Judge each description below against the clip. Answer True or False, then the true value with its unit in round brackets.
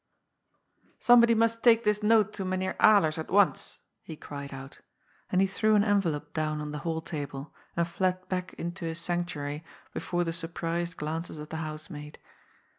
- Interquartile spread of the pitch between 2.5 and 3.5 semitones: False (4.2 semitones)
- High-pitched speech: False (170 Hz)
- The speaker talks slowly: False (175 wpm)